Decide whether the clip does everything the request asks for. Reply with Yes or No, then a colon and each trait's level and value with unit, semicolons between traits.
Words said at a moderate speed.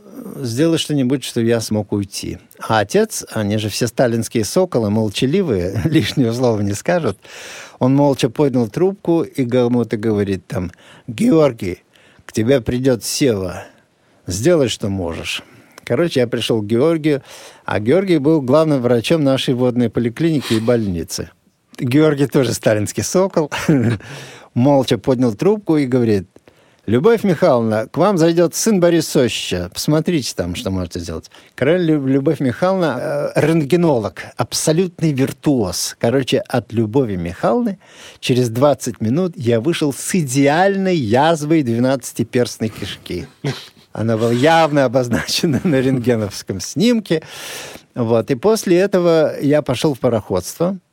Yes: average, 125 wpm